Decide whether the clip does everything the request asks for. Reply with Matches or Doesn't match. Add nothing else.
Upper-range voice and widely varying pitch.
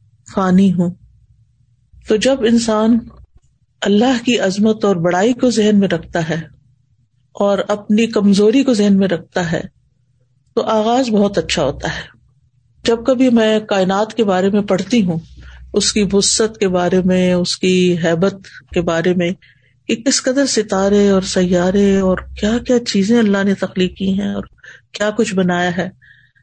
Doesn't match